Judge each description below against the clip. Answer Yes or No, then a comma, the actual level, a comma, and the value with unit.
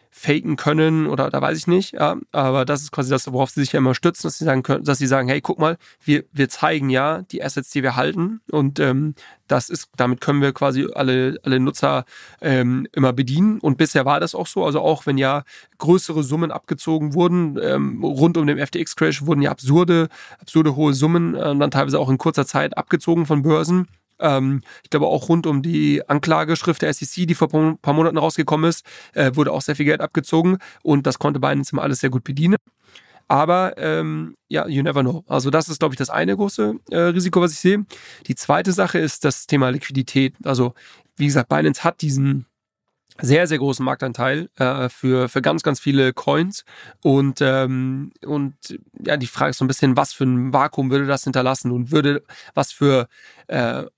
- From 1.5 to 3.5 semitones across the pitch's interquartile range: Yes, average, 3.2 semitones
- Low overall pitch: No, medium, 145 Hz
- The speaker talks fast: Yes, fast, 200 wpm